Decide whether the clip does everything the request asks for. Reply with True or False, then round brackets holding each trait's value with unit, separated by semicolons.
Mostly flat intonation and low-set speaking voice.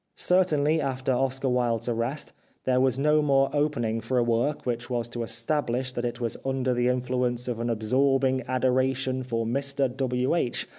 True (2.1 semitones; 130 Hz)